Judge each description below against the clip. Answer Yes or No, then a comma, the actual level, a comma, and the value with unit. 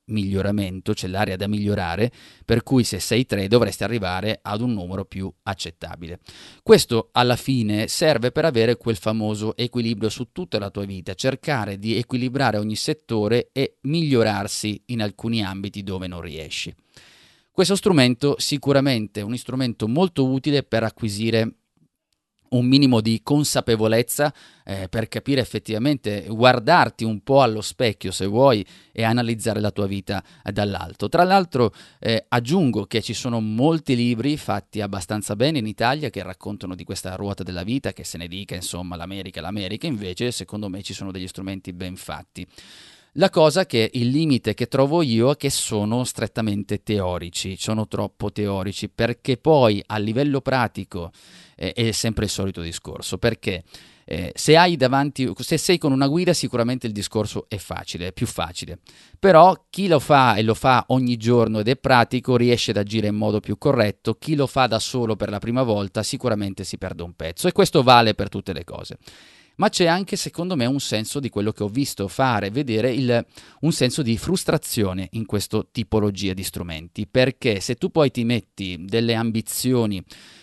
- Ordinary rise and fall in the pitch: Yes, average, 4.3 semitones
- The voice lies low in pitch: Yes, low, 115 Hz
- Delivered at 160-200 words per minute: Yes, fast, 170 wpm